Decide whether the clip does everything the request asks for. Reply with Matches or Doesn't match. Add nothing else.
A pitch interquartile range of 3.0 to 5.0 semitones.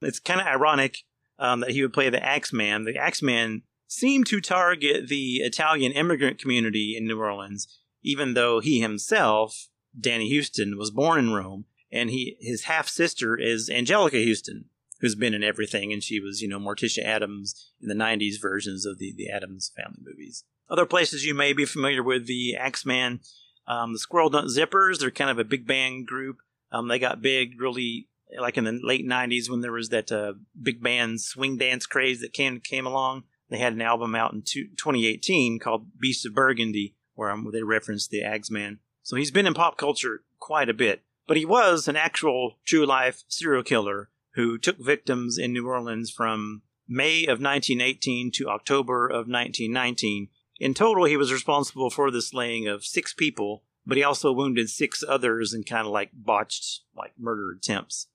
Matches